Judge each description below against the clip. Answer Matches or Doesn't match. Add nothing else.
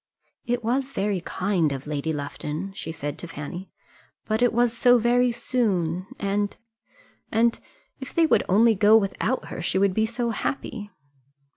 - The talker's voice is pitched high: Matches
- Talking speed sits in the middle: Matches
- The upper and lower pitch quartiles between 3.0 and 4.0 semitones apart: Doesn't match